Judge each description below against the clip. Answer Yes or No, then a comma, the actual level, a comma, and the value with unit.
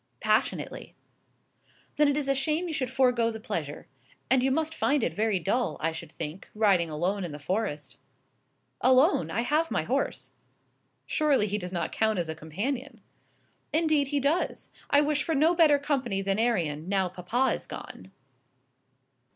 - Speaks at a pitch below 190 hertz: No, high, 230 Hz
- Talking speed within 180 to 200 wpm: No, average, 165 wpm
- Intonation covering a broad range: Yes, wide, 8.0 semitones